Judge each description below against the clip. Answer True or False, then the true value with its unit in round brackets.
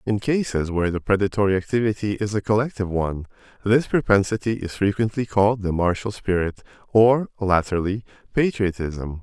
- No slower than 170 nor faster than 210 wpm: False (135 wpm)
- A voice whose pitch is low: True (100 Hz)